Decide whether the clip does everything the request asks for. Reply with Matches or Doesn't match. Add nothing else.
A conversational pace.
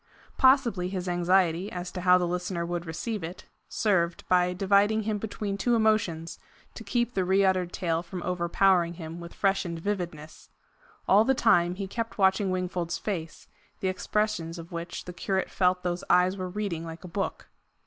Matches